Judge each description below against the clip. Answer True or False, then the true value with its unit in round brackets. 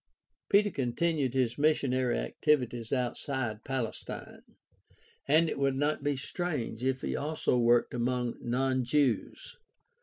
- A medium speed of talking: False (120 wpm)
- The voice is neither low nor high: False (130 Hz)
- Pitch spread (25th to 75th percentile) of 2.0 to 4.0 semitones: True (3.1 semitones)